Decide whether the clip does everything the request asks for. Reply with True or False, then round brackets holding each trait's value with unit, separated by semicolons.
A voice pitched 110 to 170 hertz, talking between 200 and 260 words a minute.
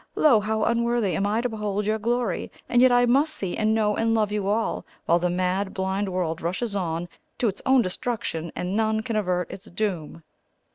False (210 Hz; 205 wpm)